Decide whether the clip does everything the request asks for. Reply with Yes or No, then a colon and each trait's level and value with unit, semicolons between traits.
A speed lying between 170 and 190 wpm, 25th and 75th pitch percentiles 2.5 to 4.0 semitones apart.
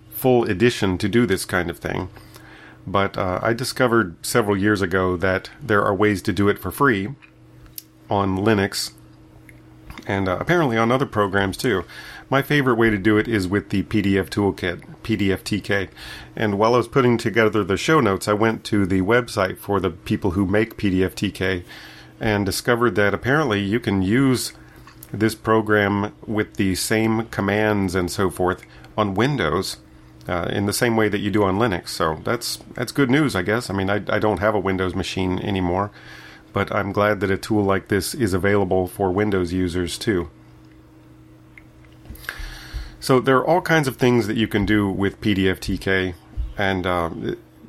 Yes: average, 175 wpm; average, 3.1 semitones